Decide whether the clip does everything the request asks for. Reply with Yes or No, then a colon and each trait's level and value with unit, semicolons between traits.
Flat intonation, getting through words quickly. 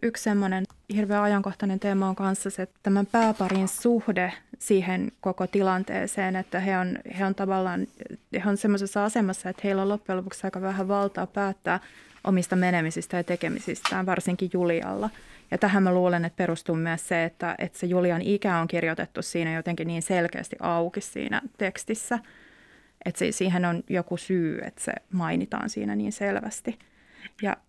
Yes: narrow, 2.3 semitones; fast, 165 wpm